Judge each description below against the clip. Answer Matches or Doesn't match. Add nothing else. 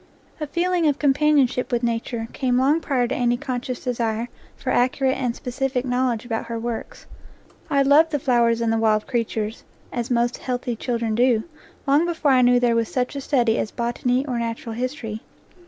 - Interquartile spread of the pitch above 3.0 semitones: Doesn't match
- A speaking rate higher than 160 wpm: Matches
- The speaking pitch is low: Doesn't match